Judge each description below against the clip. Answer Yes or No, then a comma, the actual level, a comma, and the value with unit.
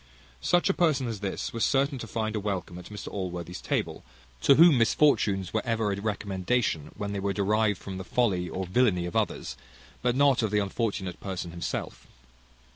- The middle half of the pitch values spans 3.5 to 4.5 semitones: Yes, average, 4.2 semitones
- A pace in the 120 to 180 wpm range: No, average, 190 wpm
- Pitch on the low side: Yes, low, 105 Hz